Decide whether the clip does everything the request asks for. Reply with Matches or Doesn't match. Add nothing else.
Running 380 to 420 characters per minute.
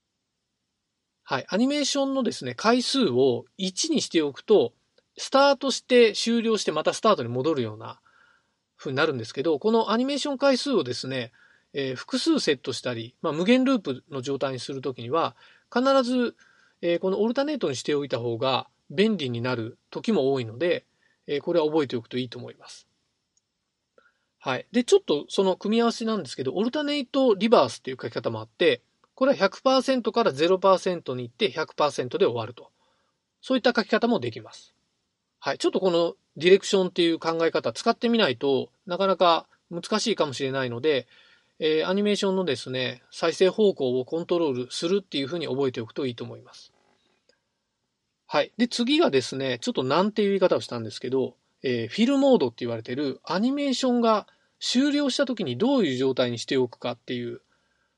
Matches